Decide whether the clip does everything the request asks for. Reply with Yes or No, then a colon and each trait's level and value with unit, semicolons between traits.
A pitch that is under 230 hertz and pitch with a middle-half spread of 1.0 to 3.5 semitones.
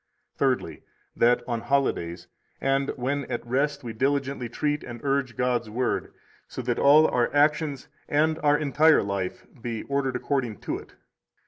Yes: low, 135 Hz; average, 3.2 semitones